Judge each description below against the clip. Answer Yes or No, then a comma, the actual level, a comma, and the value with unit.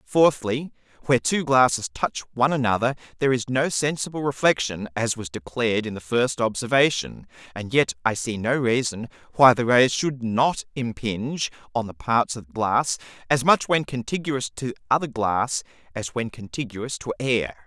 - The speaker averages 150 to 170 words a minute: Yes, average, 165 wpm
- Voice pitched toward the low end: Yes, low, 120 Hz